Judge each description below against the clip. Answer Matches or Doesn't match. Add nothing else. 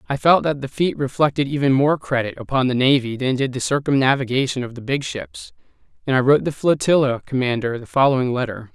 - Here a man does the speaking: Matches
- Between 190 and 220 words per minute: Matches